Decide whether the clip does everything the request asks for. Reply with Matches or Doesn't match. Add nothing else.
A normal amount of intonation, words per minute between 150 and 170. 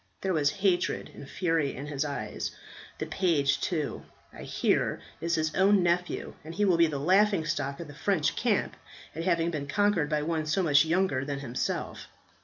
Doesn't match